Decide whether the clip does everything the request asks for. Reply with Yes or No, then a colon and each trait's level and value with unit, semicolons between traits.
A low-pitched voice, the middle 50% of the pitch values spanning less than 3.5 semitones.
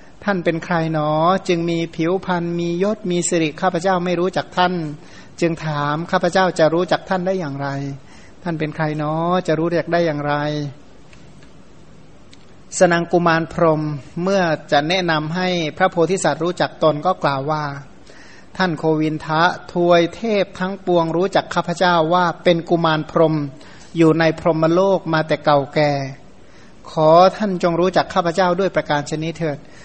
No: medium, 165 Hz; average, 2.7 semitones